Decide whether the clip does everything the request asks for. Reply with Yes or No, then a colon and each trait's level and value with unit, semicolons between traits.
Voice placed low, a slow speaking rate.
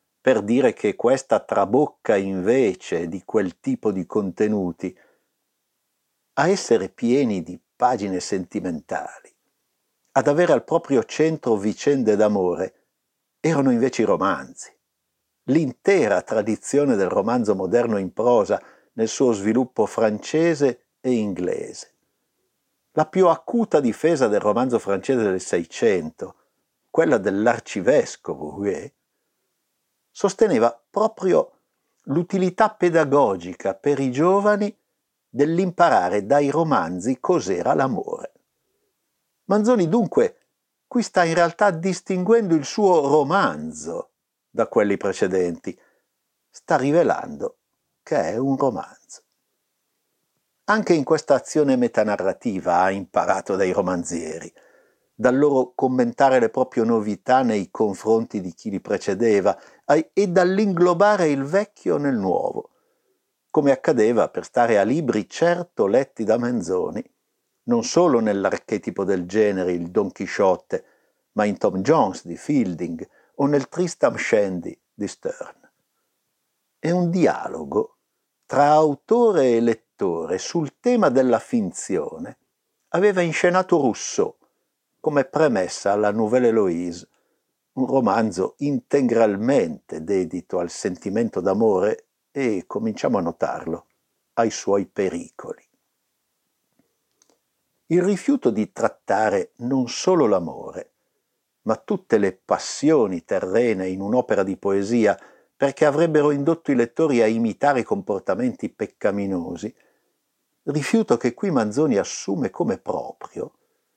No: medium, 150 Hz; slow, 110 wpm